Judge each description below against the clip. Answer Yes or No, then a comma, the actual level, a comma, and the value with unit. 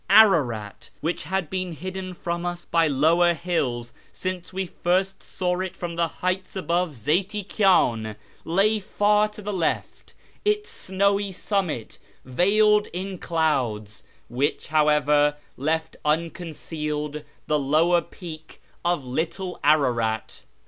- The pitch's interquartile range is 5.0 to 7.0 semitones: No, average, 4.0 semitones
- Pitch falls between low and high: Yes, medium, 170 Hz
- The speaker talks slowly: Yes, slow, 120 wpm